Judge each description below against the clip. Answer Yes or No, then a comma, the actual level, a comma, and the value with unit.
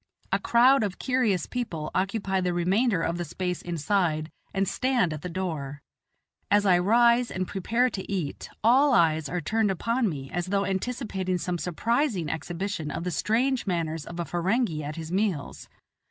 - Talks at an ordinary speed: Yes, average, 170 wpm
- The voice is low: No, medium, 185 Hz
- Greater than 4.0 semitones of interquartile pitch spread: Yes, average, 5.1 semitones